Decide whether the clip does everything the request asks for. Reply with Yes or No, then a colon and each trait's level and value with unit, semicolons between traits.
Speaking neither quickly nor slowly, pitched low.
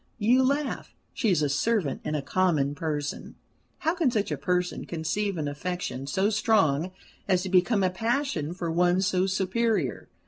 No: average, 170 wpm; medium, 185 Hz